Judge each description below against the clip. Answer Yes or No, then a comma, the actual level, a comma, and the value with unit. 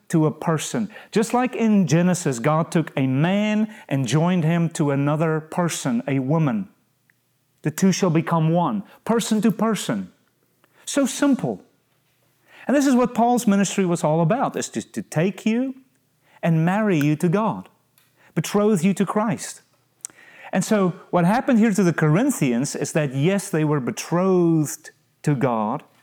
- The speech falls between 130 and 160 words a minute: Yes, average, 155 wpm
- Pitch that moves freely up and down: Yes, wide, 5.8 semitones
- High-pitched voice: No, medium, 175 Hz